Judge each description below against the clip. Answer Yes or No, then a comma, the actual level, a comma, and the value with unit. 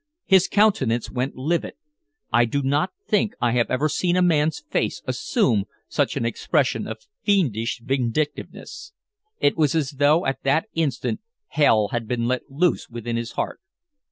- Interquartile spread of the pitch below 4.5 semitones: No, wide, 5.5 semitones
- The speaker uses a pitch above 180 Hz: No, low, 135 Hz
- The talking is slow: No, average, 155 wpm